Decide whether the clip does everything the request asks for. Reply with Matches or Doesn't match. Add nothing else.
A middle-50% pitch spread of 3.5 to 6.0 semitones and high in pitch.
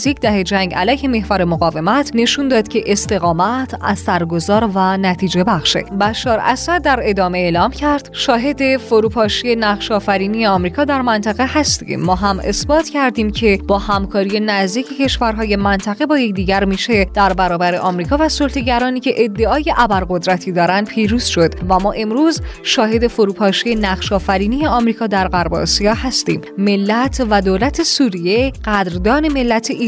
Matches